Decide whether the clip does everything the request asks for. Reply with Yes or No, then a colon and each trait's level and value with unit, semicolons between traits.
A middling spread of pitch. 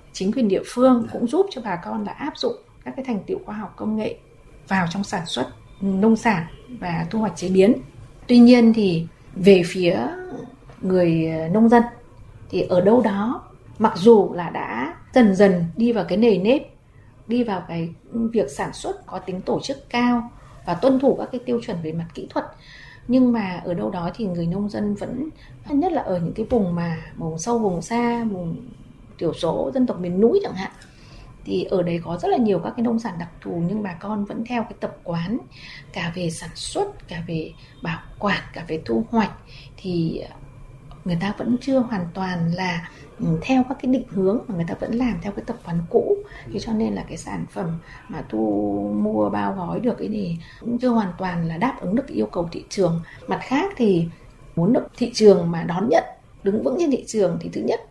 No: wide, 5.8 semitones